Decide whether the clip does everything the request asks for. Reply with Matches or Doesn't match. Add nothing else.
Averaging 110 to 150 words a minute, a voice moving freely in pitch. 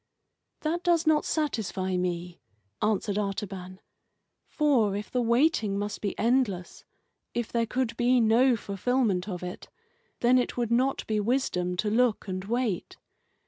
Doesn't match